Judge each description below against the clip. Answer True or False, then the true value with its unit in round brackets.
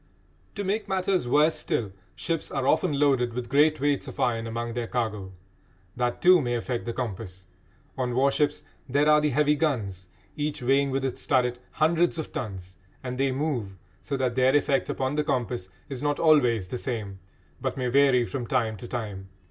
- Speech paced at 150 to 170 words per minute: False (185 wpm)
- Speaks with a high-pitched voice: False (130 Hz)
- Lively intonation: False (3.9 semitones)